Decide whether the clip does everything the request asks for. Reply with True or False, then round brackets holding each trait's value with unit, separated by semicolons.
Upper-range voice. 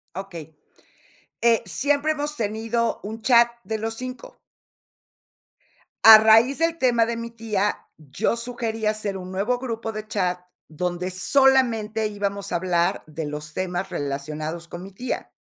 True (215 Hz)